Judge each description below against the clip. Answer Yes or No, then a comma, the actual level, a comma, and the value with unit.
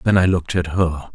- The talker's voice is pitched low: Yes, very low, 85 Hz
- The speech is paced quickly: Yes, fast, 260 wpm